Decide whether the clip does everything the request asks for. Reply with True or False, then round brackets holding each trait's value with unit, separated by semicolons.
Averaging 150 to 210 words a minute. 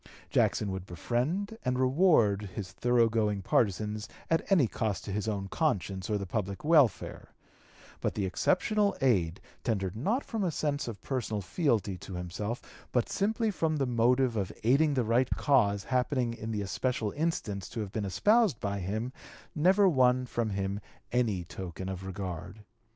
True (165 wpm)